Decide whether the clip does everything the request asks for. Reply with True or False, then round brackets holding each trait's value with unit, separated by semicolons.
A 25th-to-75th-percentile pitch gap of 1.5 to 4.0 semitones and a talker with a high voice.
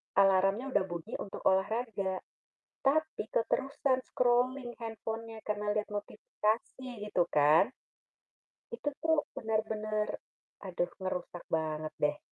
False (4.4 semitones; 215 Hz)